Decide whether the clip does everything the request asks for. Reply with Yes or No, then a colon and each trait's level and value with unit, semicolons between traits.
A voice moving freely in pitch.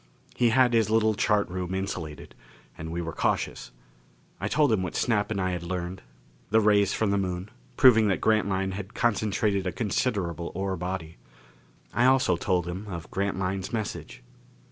No: average, 3.1 semitones